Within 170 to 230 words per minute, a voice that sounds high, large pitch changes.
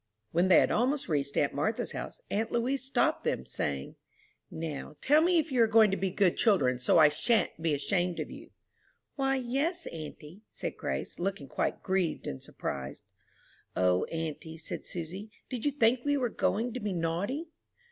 Yes: average, 180 wpm; high, 195 Hz; wide, 8.0 semitones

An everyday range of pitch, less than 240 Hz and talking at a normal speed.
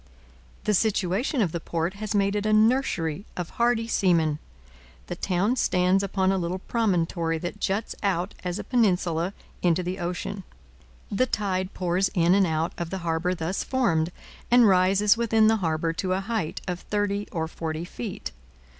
Yes: average, 3.3 semitones; medium, 185 Hz; average, 170 wpm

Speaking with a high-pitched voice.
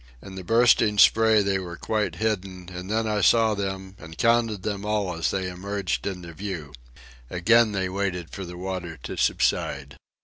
No: very low, 95 Hz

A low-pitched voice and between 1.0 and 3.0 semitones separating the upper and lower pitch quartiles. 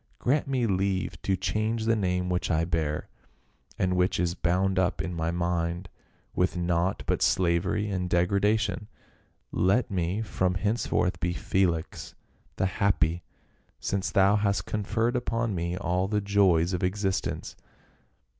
Yes: very low, 95 Hz; average, 2.7 semitones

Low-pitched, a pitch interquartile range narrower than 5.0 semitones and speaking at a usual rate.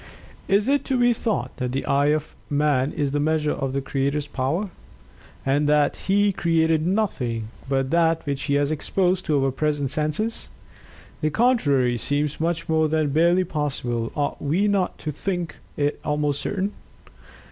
No: medium, 150 Hz; average, 3.7 semitones; average, 165 wpm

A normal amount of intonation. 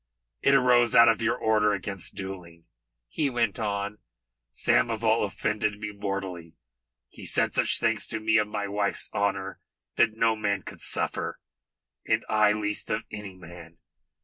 No: narrow, 2.1 semitones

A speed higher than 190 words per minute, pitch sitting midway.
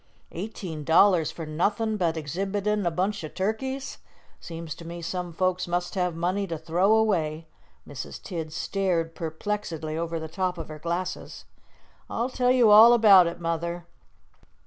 No: average, 155 wpm; medium, 175 Hz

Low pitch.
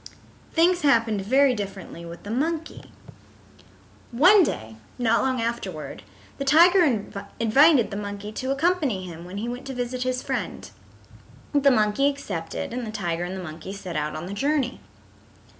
No: high, 230 Hz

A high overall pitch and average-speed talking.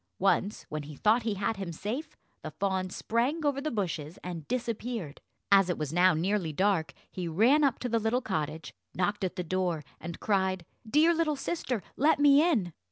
Yes: high, 200 Hz; average, 190 wpm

